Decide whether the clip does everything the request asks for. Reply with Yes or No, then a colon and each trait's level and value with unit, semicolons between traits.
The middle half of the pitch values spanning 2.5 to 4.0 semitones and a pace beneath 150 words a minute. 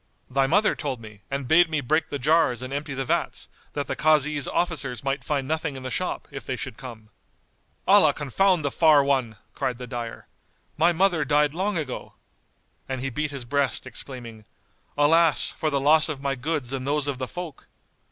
No: average, 3.2 semitones; average, 195 wpm